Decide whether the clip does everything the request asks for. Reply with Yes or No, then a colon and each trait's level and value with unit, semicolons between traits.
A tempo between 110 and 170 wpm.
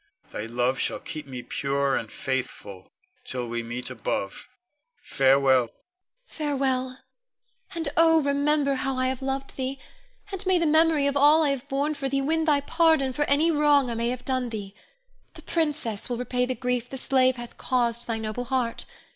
No: average, 180 wpm